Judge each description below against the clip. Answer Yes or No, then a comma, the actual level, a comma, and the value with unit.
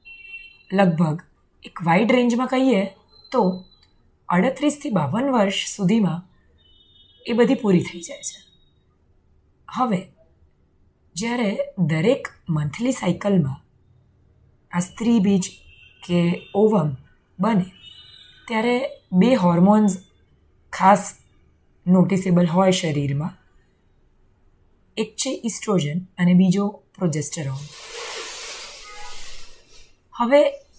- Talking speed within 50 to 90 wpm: Yes, average, 80 wpm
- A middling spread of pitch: No, wide, 8.3 semitones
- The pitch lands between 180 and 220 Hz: Yes, medium, 185 Hz